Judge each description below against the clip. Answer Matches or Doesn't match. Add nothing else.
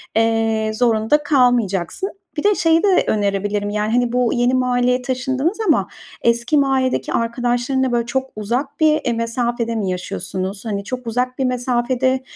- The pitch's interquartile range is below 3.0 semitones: Matches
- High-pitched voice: Matches